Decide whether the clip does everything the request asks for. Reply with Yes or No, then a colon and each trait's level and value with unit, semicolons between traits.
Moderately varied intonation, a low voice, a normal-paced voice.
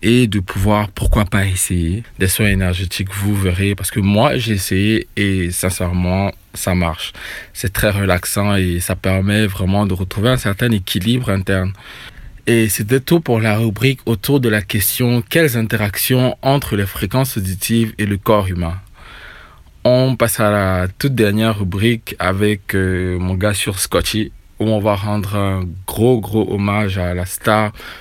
Yes: average, 3.0 semitones; low, 105 Hz; average, 165 wpm